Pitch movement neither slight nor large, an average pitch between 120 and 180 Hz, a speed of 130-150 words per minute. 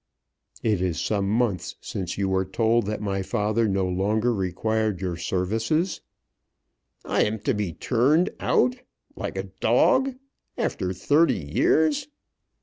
No: average, 3.7 semitones; low, 105 Hz; slow, 135 wpm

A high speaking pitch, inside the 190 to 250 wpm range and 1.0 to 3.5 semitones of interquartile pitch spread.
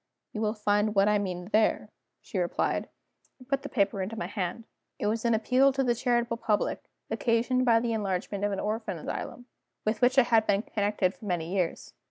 Yes: high, 215 Hz; fast, 205 wpm; average, 2.9 semitones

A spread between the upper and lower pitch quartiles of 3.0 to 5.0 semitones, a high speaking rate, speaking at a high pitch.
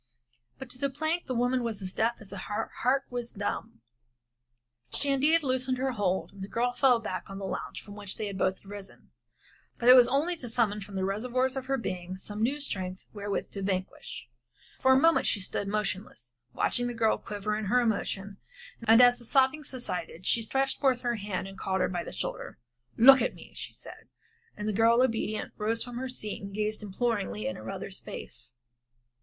Yes: average, 4.3 semitones; fast, 210 wpm; high, 225 Hz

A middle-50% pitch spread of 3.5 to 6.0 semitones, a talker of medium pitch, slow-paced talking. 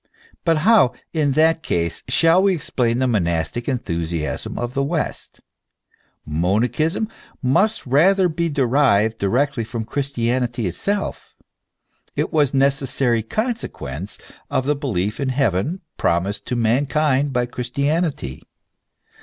No: wide, 5.4 semitones; low, 130 Hz; slow, 120 wpm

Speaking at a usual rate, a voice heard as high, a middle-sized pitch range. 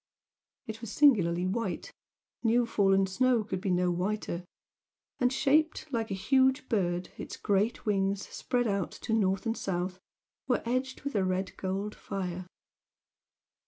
Yes: average, 145 wpm; high, 205 Hz; average, 4.4 semitones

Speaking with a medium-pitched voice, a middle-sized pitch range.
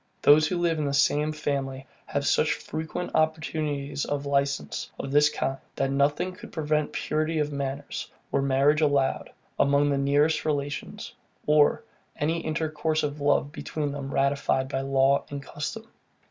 No: medium, 145 Hz; narrow, 1.7 semitones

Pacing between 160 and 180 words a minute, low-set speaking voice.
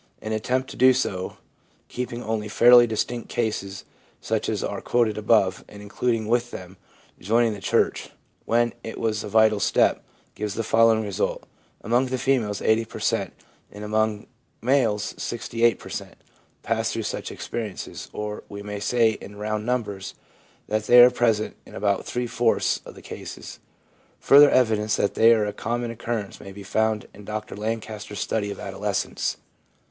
Yes: average, 170 wpm; low, 110 Hz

